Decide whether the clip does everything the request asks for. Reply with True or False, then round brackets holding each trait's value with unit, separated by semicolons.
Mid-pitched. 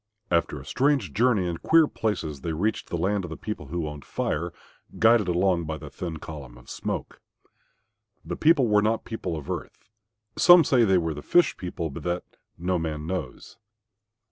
False (90 Hz)